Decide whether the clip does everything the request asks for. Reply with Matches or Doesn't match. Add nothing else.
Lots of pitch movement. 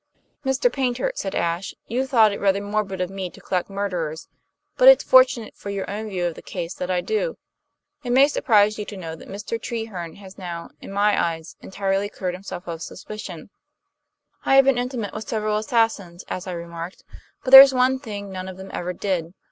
Doesn't match